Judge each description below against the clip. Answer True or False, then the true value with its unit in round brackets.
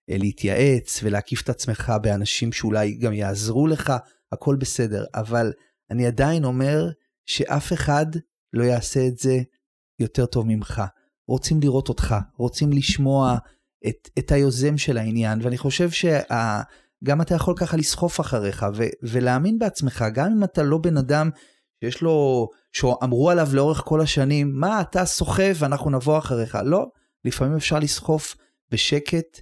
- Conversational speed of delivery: True (140 wpm)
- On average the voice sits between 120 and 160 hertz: True (135 Hz)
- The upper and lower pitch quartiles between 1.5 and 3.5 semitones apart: False (4.6 semitones)